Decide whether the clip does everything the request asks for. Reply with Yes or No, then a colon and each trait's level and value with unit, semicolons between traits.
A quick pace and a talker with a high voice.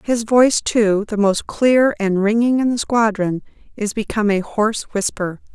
No: average, 175 wpm; high, 215 Hz